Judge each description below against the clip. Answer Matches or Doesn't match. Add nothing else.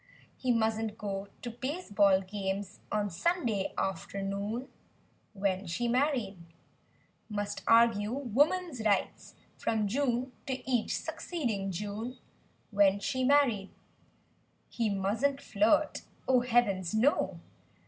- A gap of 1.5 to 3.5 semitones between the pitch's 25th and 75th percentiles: Doesn't match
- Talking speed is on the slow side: Matches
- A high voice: Matches